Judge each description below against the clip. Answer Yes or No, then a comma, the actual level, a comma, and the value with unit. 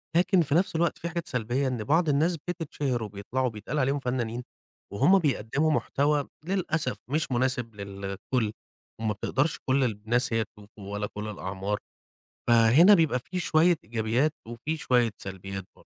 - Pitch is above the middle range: No, low, 125 Hz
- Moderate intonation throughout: No, wide, 6.1 semitones